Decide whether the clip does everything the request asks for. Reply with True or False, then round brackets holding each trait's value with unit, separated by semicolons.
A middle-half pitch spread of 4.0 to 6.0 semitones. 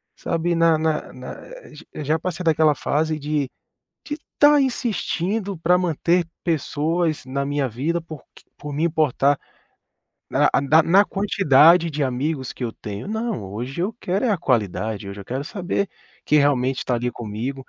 True (4.6 semitones)